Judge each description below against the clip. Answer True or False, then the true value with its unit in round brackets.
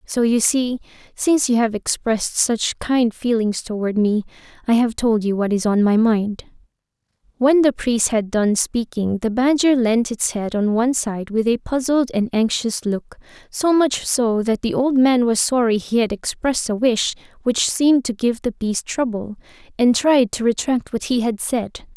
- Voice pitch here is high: True (235 Hz)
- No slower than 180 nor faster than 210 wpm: True (190 wpm)